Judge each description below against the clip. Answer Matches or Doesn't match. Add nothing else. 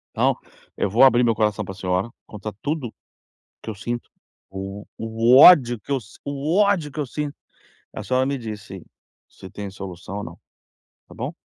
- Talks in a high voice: Doesn't match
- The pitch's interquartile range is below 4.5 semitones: Doesn't match